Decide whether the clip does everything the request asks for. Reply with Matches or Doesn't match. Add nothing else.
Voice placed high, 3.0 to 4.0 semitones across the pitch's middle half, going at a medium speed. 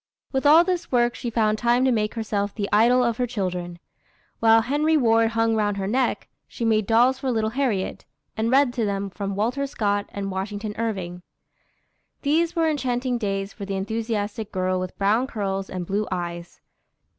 Matches